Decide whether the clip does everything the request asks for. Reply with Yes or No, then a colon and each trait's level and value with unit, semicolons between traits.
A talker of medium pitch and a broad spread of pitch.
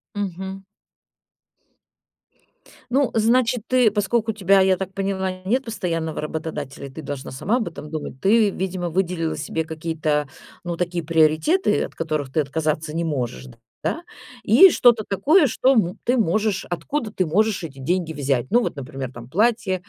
Yes: medium, 180 Hz; wide, 5.7 semitones